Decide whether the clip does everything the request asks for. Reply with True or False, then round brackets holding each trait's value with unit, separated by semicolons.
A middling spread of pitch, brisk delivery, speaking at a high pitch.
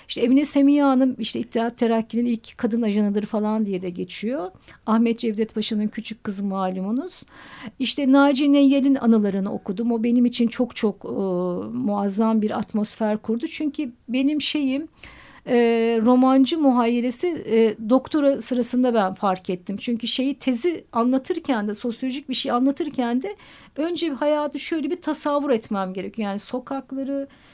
True (3.9 semitones; 145 wpm; 240 Hz)